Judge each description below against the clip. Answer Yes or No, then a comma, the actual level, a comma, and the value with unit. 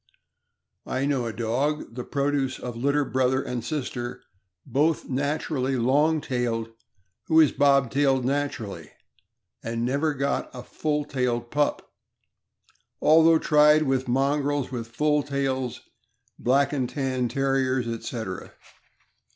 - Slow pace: Yes, slow, 120 wpm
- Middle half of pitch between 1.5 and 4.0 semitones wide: Yes, average, 2.7 semitones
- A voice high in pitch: No, low, 135 Hz